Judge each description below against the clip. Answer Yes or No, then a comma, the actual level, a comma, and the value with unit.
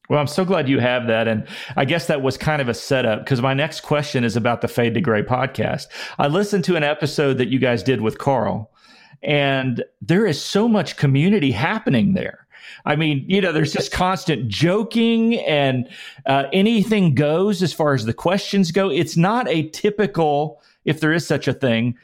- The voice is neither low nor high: Yes, medium, 150 Hz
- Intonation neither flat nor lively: No, wide, 6.0 semitones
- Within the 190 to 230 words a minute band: Yes, average, 200 wpm